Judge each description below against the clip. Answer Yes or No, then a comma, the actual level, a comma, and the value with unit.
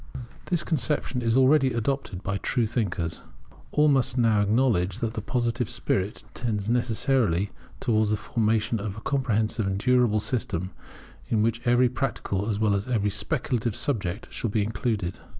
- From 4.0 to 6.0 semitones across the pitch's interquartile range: No, average, 3.3 semitones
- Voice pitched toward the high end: No, low, 115 Hz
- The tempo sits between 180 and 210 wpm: No, average, 155 wpm